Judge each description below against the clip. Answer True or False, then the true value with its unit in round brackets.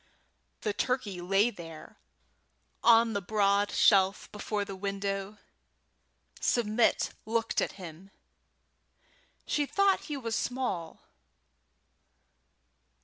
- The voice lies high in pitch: True (205 Hz)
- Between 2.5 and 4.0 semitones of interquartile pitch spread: True (2.9 semitones)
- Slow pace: True (90 wpm)